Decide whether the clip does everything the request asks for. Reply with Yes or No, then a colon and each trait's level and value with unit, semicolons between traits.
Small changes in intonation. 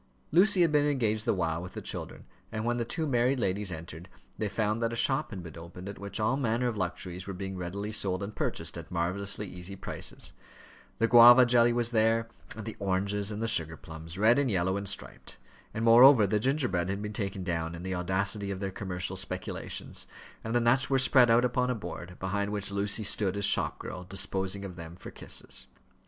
No: average, 4.1 semitones